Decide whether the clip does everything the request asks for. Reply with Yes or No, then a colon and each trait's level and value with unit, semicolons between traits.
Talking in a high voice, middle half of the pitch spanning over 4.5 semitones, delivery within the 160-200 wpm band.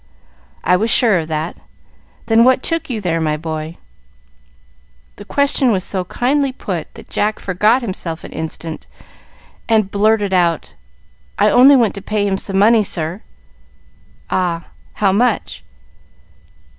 No: high, 200 Hz; average, 5.1 semitones; average, 140 wpm